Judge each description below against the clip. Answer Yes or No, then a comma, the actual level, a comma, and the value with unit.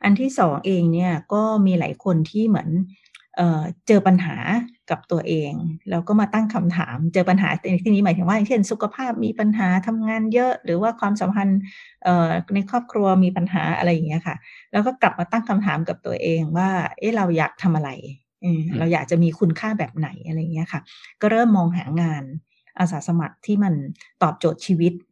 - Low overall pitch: No, medium, 185 Hz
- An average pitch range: Yes, average, 3.7 semitones